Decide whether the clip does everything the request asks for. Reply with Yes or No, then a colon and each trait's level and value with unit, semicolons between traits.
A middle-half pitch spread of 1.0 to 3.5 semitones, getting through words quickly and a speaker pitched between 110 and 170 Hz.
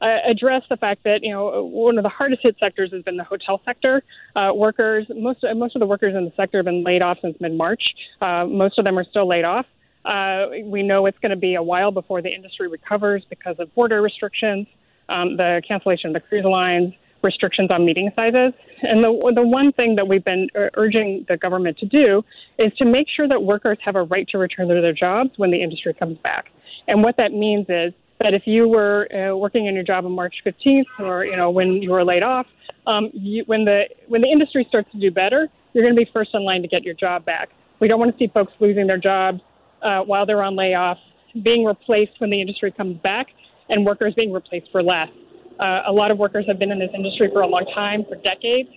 No: average, 3.2 semitones; fast, 240 wpm; high, 200 Hz